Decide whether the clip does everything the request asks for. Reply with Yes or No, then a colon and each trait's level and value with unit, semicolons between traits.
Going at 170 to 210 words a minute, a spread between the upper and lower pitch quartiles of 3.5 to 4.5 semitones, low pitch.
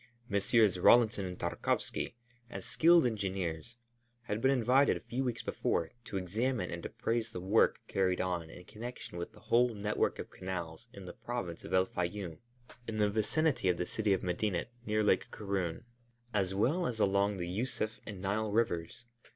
Yes: average, 175 wpm; average, 4.2 semitones; low, 100 Hz